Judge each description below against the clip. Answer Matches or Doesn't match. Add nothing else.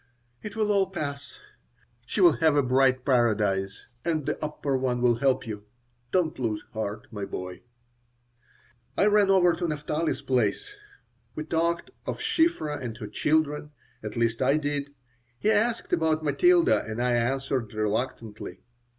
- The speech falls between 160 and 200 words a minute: Doesn't match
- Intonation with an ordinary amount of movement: Doesn't match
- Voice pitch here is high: Doesn't match